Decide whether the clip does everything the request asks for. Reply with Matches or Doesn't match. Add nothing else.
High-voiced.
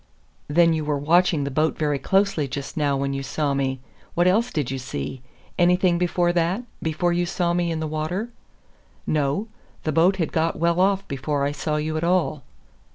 Doesn't match